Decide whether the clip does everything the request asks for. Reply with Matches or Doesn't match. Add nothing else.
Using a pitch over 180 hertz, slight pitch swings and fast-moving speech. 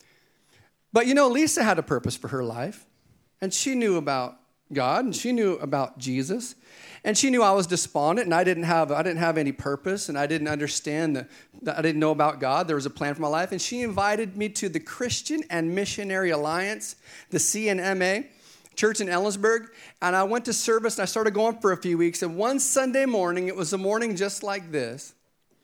Doesn't match